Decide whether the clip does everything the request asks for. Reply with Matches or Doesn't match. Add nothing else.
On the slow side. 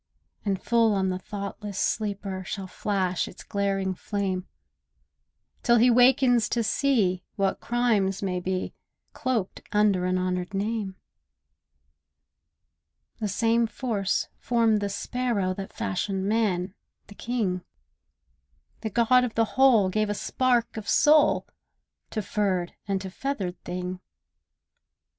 Matches